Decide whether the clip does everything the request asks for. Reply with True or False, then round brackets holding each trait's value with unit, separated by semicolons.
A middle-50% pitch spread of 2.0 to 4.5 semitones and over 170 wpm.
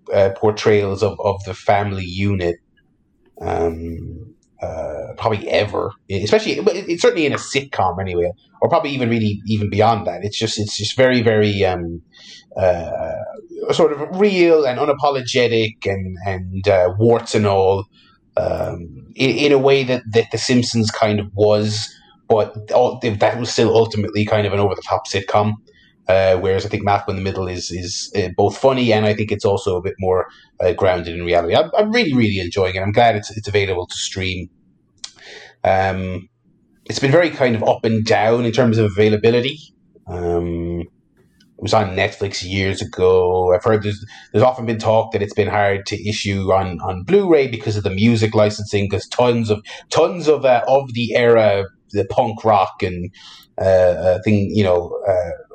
True (3.5 semitones; 180 wpm)